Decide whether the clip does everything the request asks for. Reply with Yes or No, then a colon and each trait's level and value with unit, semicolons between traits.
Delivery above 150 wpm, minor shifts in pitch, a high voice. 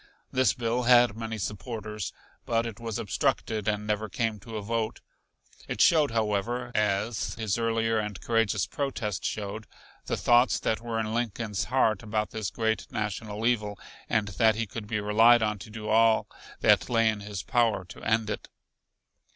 No: average, 170 wpm; narrow, 1.6 semitones; low, 110 Hz